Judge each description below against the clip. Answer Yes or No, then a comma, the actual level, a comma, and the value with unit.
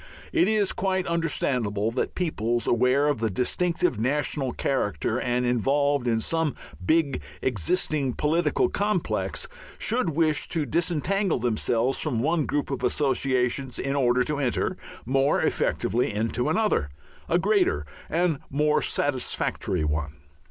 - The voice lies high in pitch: No, medium, 140 Hz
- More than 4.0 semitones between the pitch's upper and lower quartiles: Yes, average, 5.3 semitones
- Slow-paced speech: Yes, slow, 130 wpm